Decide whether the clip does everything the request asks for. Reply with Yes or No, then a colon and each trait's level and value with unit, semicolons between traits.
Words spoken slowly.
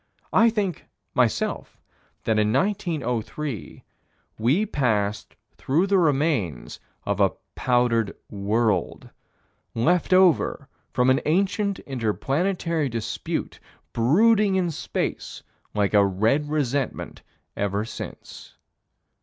Yes: slow, 100 wpm